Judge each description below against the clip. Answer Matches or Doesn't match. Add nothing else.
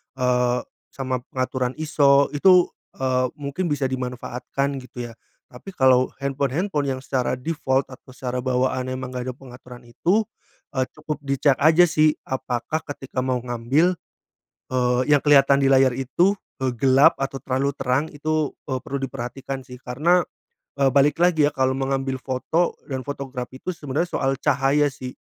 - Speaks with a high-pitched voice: Doesn't match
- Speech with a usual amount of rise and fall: Doesn't match